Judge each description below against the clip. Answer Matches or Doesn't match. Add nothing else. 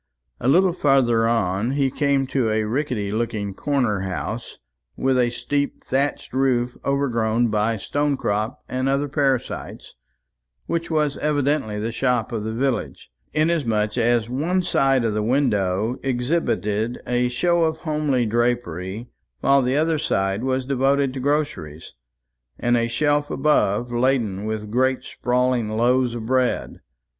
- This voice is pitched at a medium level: Doesn't match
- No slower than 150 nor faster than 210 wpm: Doesn't match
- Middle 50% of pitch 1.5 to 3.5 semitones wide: Doesn't match